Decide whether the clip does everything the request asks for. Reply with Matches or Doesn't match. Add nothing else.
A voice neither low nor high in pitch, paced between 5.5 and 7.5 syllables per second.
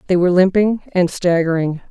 Matches